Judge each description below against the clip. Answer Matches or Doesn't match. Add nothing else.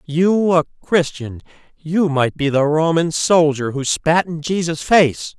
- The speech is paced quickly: Doesn't match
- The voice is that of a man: Matches